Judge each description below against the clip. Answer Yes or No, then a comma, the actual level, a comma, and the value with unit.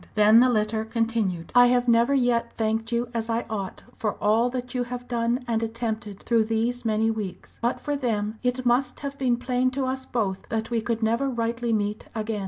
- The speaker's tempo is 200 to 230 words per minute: Yes, fast, 205 wpm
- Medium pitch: No, high, 230 Hz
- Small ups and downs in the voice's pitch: Yes, narrow, 1.9 semitones